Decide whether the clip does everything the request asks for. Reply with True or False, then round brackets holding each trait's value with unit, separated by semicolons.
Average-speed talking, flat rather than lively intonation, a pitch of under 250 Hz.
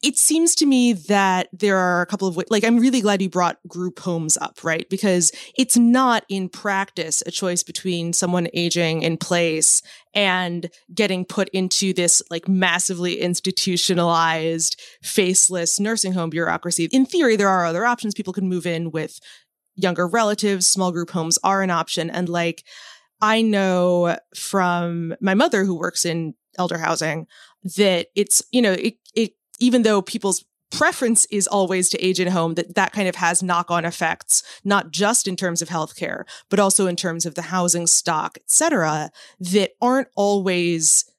False (175 wpm; 3.0 semitones; 185 Hz)